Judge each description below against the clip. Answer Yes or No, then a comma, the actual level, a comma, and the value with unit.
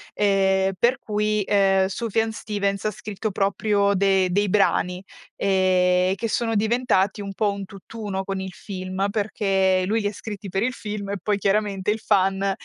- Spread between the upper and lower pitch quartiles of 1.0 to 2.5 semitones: Yes, narrow, 1.7 semitones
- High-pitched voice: Yes, high, 200 Hz